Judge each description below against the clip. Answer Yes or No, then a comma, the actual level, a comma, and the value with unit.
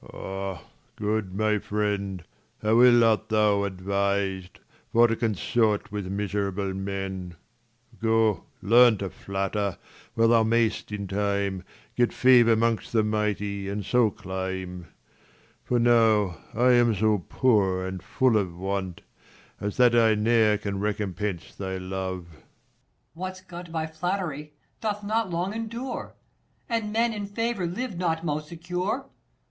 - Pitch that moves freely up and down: No, average, 4.5 semitones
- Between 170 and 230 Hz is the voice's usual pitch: No, low, 110 Hz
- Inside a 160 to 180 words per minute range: No, average, 145 wpm